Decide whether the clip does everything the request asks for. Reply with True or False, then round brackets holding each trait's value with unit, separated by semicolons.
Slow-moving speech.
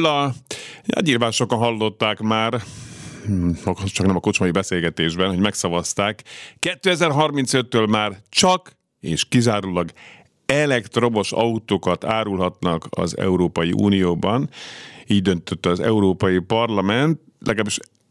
True (95 wpm)